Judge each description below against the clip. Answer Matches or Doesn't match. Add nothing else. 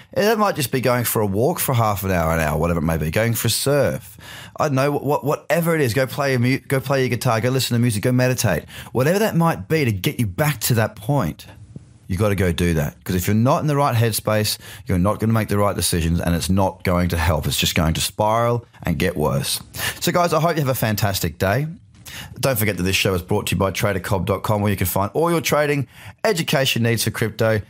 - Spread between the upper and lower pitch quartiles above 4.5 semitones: Matches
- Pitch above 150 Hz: Doesn't match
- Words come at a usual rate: Doesn't match